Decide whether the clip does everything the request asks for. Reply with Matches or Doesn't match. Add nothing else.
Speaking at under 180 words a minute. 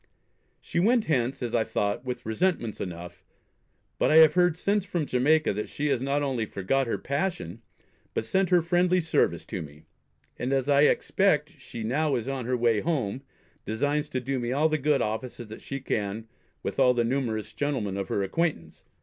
Doesn't match